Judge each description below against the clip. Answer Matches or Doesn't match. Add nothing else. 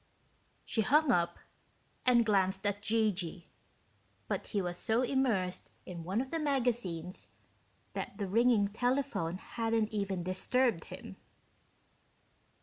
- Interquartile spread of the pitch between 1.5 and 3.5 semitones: Doesn't match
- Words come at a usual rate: Doesn't match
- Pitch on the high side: Matches